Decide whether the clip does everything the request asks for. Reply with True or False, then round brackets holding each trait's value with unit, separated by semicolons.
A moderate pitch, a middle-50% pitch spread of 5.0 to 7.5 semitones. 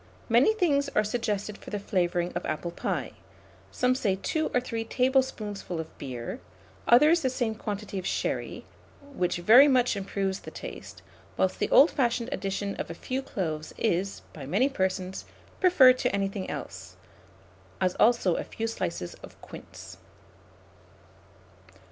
False (205 Hz; 5.6 semitones)